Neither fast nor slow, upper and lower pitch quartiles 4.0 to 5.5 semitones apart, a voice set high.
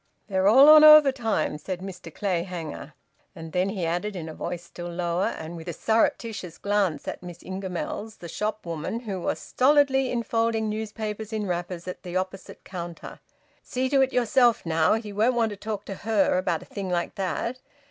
Yes: average, 185 wpm; average, 4.3 semitones; high, 195 Hz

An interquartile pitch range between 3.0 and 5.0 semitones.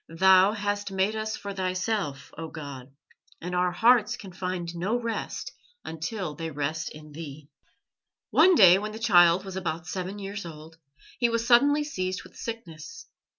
Yes: average, 4.7 semitones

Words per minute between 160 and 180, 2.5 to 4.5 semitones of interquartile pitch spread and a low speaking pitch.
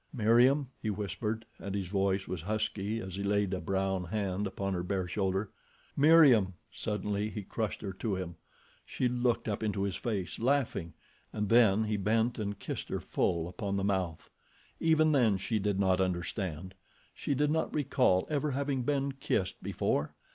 Yes: average, 170 wpm; average, 3.9 semitones; low, 105 Hz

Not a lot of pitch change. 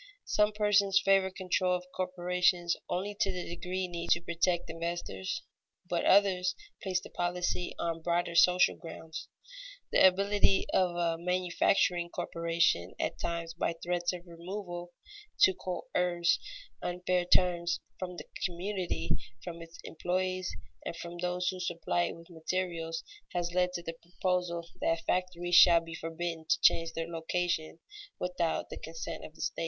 Yes: narrow, 1.3 semitones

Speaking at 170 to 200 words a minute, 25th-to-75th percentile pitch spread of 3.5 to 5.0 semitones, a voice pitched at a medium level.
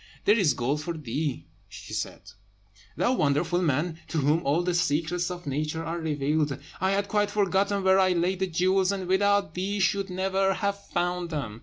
Yes: average, 185 wpm; average, 4.0 semitones; medium, 175 Hz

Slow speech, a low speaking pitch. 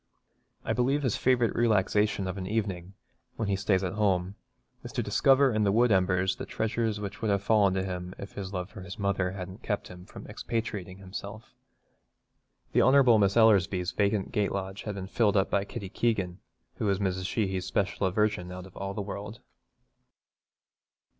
No: average, 185 wpm; low, 100 Hz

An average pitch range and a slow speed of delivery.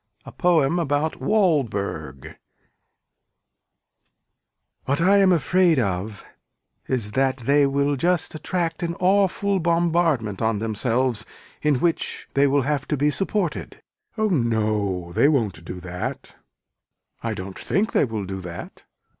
No: wide, 7.9 semitones; slow, 130 wpm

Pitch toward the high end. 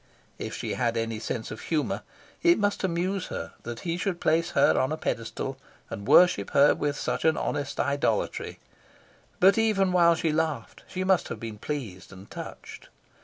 No: medium, 150 Hz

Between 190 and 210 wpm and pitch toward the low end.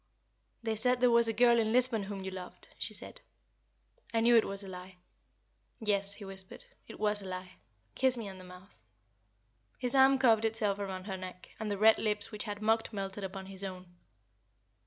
No: average, 200 wpm; high, 205 Hz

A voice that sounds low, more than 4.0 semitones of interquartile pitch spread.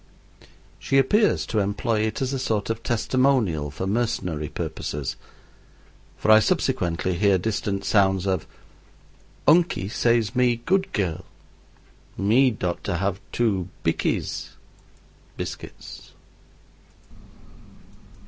Yes: low, 105 Hz; average, 4.4 semitones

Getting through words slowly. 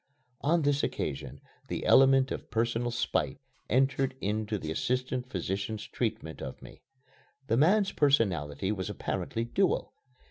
Yes: slow, 130 wpm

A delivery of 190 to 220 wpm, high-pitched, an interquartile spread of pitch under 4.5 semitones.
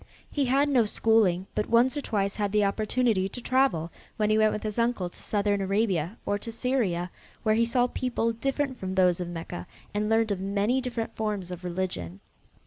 Yes: average, 200 wpm; high, 210 Hz; average, 3.9 semitones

